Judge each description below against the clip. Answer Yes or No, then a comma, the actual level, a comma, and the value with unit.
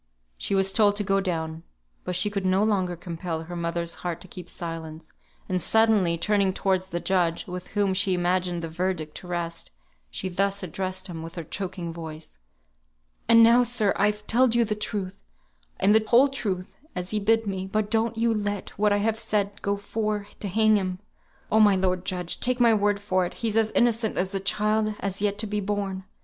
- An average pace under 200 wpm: No, fast, 205 wpm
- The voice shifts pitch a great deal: No, average, 2.9 semitones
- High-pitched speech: Yes, high, 195 Hz